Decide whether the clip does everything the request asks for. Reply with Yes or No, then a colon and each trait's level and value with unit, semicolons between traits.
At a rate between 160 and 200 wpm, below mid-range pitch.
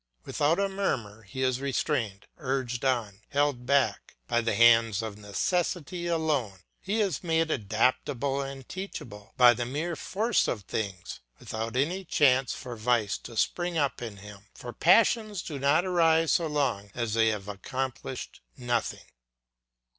No: average, 150 wpm; low, 130 Hz